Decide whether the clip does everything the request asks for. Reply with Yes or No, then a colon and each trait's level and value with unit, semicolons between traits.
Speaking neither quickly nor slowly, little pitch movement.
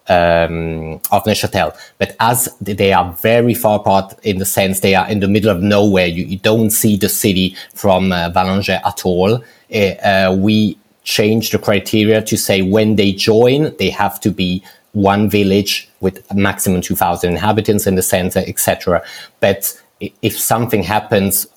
Yes: average, 170 wpm; narrow, 2.2 semitones